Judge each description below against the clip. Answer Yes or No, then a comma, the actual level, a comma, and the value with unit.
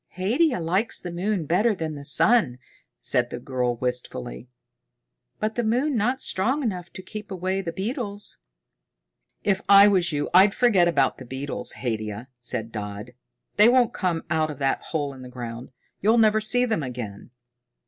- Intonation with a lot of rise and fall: Yes, wide, 8.8 semitones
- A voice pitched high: No, medium, 175 Hz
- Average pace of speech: Yes, average, 170 wpm